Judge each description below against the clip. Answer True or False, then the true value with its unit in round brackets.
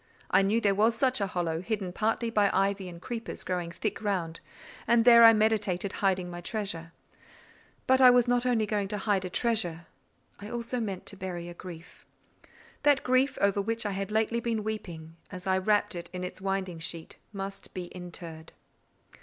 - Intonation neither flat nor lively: True (3.8 semitones)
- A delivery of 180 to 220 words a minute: True (185 wpm)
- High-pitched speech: True (200 Hz)